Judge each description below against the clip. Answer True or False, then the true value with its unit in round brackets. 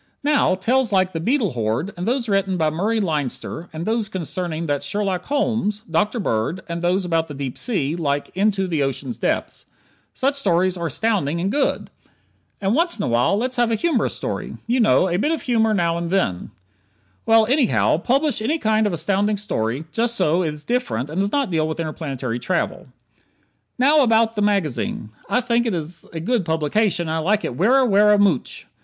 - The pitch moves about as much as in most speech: False (5.9 semitones)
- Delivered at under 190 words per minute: False (200 wpm)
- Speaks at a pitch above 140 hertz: True (190 Hz)